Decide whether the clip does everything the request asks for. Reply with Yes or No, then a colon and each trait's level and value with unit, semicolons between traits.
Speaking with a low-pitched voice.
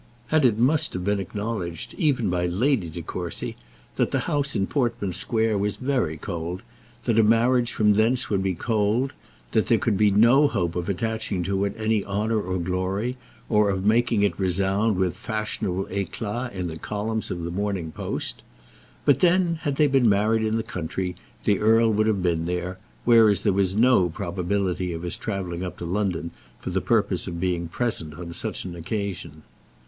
Yes: low, 100 Hz